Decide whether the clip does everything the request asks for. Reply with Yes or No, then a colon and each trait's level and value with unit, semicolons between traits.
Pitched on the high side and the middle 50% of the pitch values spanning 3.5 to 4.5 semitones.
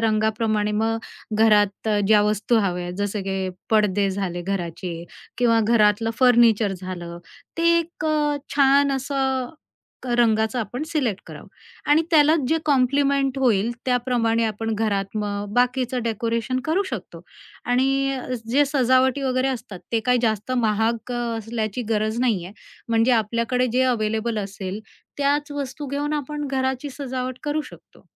Yes: high, 235 Hz; average, 3.9 semitones